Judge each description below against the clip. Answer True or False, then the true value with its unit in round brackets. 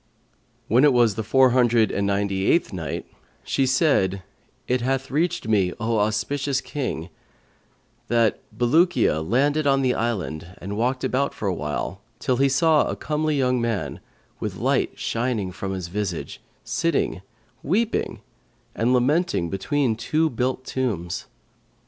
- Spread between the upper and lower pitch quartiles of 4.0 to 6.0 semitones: True (5.5 semitones)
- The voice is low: True (120 Hz)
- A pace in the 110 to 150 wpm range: True (145 wpm)